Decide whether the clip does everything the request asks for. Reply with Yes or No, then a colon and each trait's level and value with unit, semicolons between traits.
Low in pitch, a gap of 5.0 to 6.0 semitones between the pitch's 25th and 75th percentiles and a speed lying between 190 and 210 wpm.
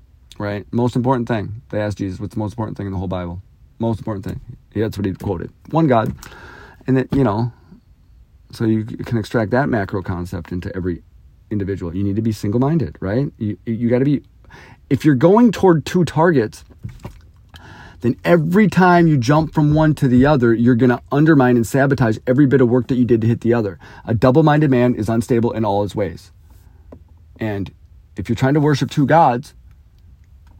Yes: low, 115 Hz; average, 5.3 semitones; average, 200 wpm